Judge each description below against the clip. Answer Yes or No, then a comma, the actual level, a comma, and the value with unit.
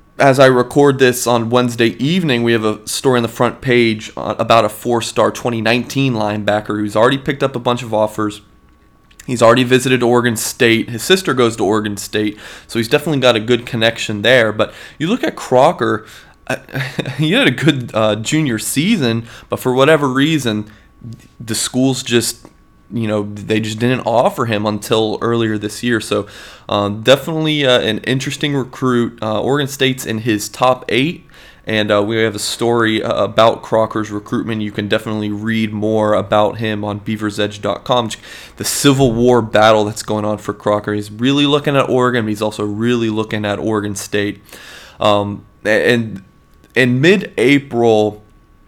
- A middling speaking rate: Yes, average, 170 wpm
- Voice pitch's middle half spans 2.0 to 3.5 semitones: Yes, average, 3.0 semitones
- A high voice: No, low, 115 Hz